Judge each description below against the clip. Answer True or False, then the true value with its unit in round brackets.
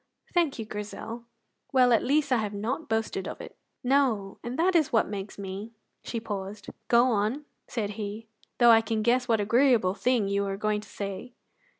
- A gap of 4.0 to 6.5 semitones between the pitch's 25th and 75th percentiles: False (3.5 semitones)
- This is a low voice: False (225 Hz)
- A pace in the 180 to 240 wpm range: True (195 wpm)